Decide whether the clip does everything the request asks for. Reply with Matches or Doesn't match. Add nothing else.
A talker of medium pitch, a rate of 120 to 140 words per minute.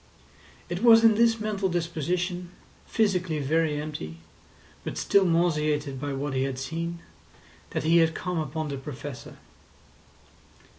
Matches